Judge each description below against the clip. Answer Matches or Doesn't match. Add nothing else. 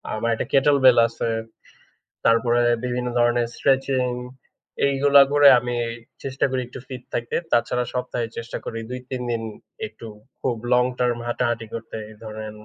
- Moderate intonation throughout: Doesn't match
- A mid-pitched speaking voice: Doesn't match